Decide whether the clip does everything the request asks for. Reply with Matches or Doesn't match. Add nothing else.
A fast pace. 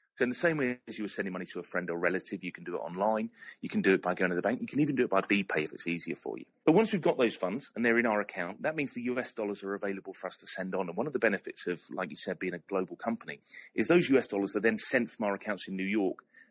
Matches